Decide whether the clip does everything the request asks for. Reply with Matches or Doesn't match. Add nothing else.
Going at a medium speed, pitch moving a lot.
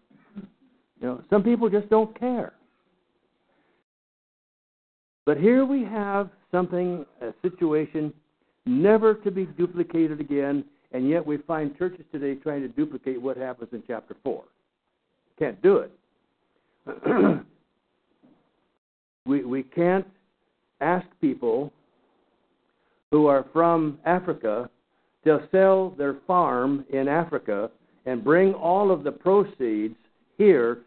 Doesn't match